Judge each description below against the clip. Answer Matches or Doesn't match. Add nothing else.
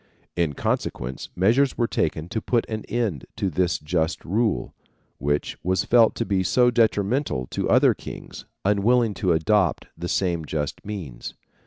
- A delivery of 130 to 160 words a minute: Matches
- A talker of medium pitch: Doesn't match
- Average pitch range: Doesn't match